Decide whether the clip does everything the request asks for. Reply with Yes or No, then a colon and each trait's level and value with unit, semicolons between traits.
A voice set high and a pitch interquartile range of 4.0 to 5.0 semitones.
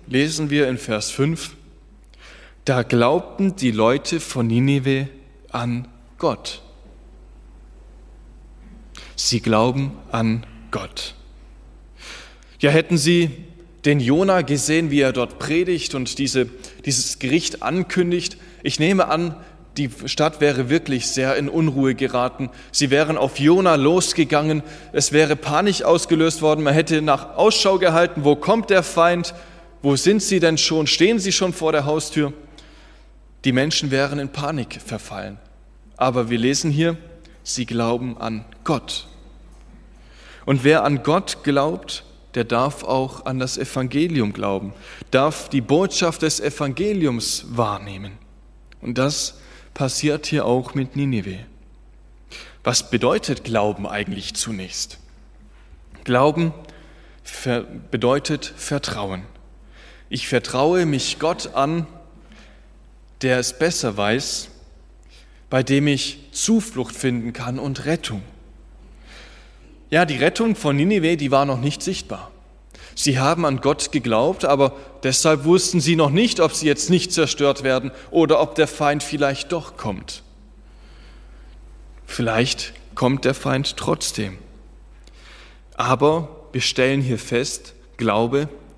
No: medium, 140 Hz; average, 4.7 semitones